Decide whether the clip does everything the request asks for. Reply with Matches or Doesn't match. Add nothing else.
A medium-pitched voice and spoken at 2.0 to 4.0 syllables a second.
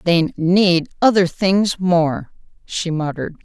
Matches